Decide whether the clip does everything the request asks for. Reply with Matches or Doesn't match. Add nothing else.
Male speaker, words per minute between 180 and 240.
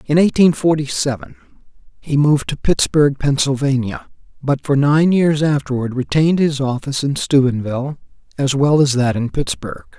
Doesn't match